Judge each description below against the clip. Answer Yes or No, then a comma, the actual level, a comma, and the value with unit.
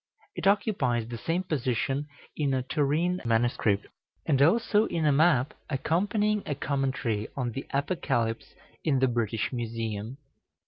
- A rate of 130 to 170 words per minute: Yes, slow, 135 wpm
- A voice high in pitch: No, low, 135 Hz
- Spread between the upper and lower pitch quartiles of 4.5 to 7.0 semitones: Yes, wide, 5.5 semitones